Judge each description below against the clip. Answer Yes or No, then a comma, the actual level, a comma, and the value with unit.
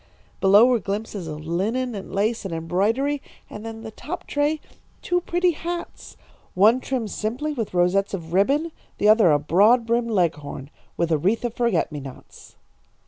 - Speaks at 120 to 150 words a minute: No, average, 170 wpm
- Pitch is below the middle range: No, high, 215 Hz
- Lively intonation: Yes, wide, 5.9 semitones